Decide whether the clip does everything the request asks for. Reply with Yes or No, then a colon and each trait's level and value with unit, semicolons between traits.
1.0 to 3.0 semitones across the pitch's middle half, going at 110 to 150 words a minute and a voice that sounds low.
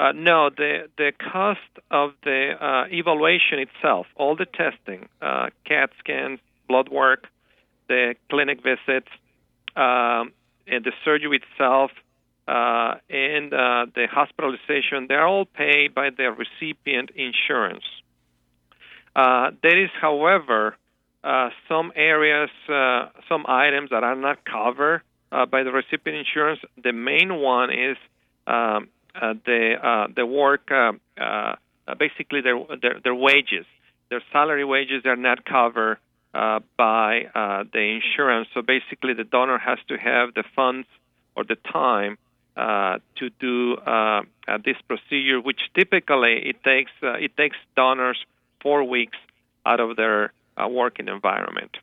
No: average, 3.8 semitones; average, 140 wpm; low, 130 Hz